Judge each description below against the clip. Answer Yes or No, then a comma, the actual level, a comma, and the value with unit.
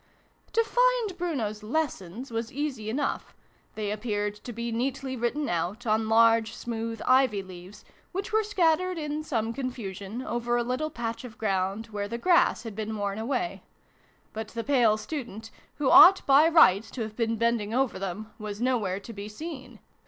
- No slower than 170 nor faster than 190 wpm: Yes, average, 180 wpm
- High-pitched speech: Yes, high, 230 Hz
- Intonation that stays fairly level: No, average, 4.5 semitones